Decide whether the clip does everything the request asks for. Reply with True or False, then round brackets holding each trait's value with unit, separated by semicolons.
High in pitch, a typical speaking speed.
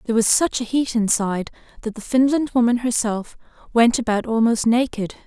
True (230 Hz; 170 wpm)